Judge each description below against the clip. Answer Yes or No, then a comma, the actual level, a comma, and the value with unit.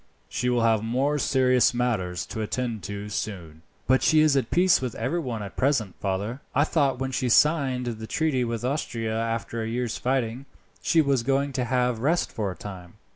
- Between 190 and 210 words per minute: Yes, average, 195 wpm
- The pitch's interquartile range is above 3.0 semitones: Yes, average, 3.4 semitones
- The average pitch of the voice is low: Yes, low, 125 Hz